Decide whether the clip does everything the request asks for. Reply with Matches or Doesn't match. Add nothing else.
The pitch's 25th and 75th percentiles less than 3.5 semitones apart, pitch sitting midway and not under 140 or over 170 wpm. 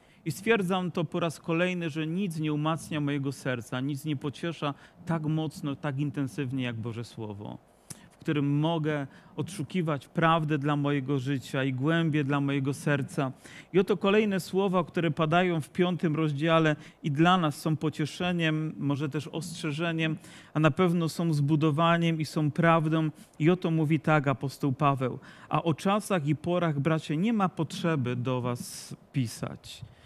Matches